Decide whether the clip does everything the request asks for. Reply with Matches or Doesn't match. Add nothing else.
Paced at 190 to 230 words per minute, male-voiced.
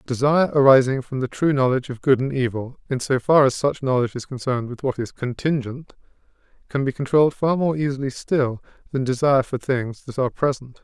Matches